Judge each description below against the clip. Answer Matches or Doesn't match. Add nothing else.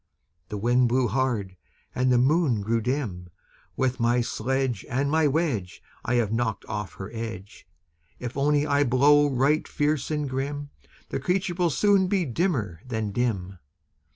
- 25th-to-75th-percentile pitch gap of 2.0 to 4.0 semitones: Doesn't match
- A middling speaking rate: Matches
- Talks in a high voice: Doesn't match